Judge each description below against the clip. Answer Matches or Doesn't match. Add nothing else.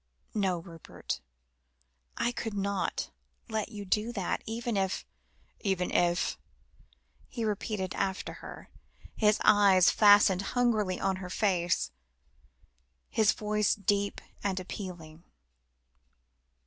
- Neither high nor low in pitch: Doesn't match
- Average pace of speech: Doesn't match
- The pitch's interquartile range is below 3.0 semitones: Matches